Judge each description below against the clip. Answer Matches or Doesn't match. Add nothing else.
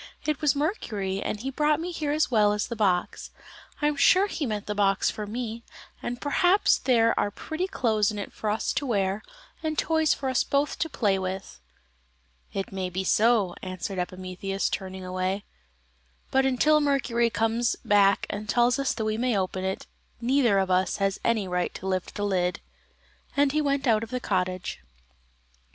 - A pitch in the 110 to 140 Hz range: Doesn't match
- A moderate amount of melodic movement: Doesn't match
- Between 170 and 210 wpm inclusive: Matches